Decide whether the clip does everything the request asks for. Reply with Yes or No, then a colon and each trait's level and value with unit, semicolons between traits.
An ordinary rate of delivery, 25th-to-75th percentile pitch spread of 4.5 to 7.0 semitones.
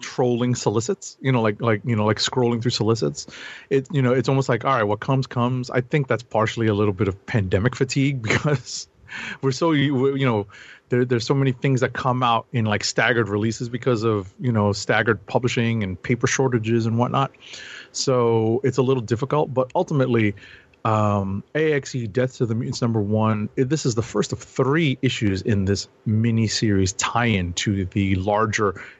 No: average, 190 wpm; average, 3.4 semitones